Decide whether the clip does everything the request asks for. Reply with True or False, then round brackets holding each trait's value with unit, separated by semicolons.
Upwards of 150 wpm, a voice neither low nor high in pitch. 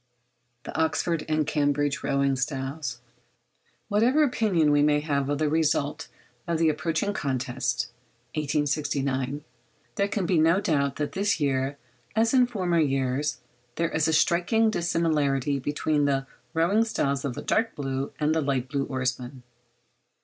False (145 wpm; 150 Hz)